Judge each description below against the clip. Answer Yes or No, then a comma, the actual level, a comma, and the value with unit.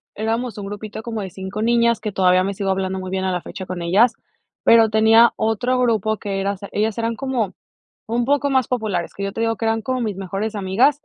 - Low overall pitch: No, high, 215 Hz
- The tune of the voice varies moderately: Yes, average, 3.2 semitones